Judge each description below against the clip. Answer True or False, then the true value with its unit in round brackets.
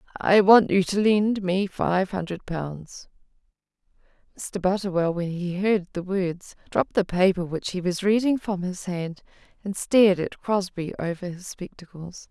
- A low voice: False (185 Hz)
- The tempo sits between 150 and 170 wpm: True (160 wpm)